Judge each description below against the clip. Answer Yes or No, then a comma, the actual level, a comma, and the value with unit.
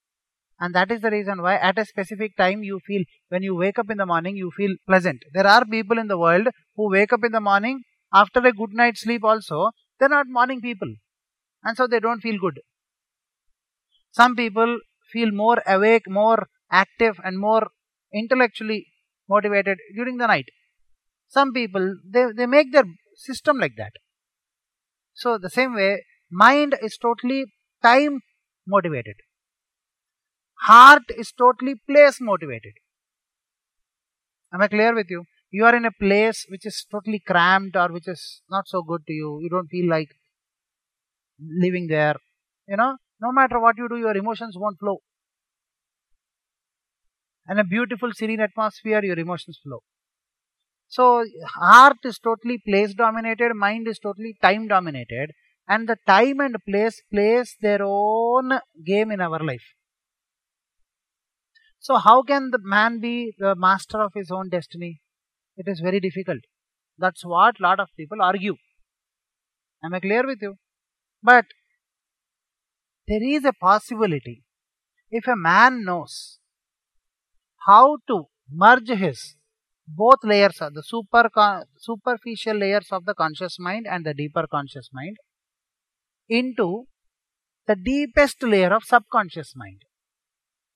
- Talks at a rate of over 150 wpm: No, average, 145 wpm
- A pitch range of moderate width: Yes, average, 4.3 semitones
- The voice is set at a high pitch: Yes, high, 210 Hz